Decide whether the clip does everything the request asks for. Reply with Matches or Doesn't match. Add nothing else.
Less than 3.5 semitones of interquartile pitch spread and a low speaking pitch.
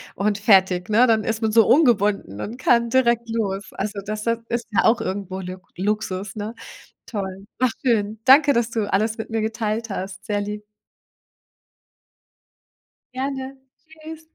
Doesn't match